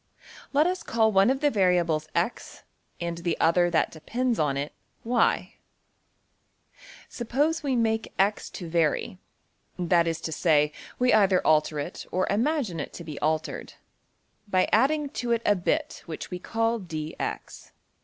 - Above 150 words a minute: No, average, 145 wpm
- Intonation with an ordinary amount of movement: No, wide, 6.3 semitones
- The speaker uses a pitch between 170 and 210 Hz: Yes, medium, 185 Hz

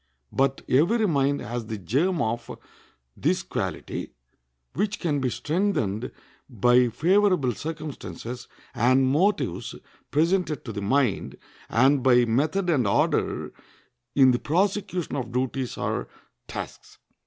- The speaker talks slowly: Yes, slow, 120 wpm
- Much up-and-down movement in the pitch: Yes, wide, 5.8 semitones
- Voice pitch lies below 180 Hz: Yes, low, 135 Hz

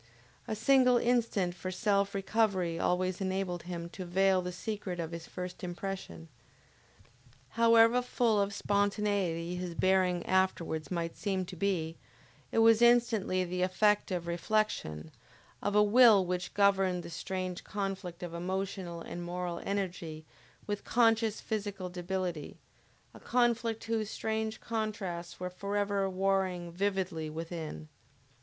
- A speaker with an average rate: No, slow, 130 wpm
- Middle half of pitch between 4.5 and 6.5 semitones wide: No, average, 3.0 semitones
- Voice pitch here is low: No, high, 190 Hz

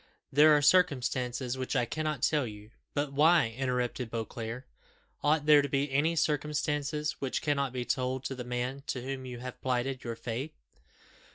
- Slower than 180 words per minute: Yes, average, 170 wpm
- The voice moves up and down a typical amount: Yes, average, 3.0 semitones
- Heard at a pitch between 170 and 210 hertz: No, low, 135 Hz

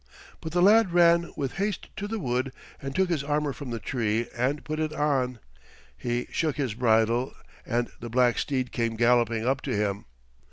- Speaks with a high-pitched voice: No, low, 130 Hz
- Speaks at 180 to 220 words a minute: Yes, average, 190 wpm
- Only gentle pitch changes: No, average, 4.6 semitones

